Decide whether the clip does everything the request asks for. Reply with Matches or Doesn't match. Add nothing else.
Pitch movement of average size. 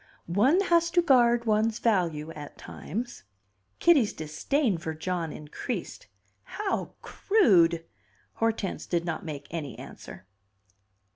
Doesn't match